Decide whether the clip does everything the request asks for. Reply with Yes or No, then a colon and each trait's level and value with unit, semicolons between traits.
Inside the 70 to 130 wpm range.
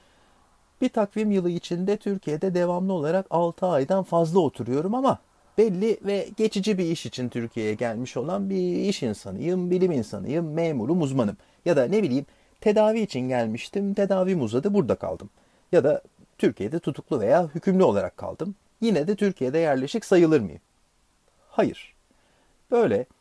No: fast, 140 wpm